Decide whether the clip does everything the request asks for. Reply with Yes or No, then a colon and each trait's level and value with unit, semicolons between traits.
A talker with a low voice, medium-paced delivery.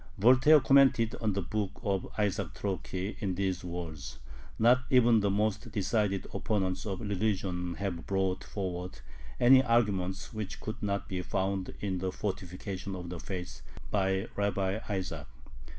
Yes: low, 100 Hz; average, 145 wpm